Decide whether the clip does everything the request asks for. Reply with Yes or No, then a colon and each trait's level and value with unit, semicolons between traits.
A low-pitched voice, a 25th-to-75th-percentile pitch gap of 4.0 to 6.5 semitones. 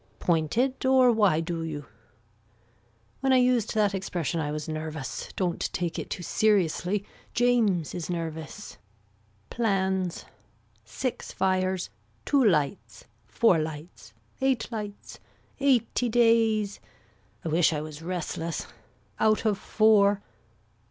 No: high, 190 Hz; wide, 5.4 semitones